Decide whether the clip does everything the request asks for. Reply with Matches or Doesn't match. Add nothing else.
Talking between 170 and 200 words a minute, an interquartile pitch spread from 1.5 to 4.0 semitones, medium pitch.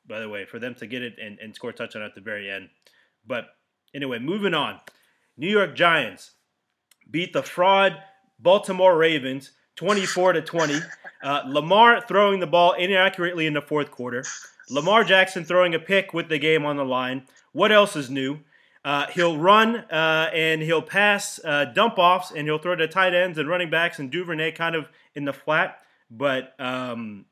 Doesn't match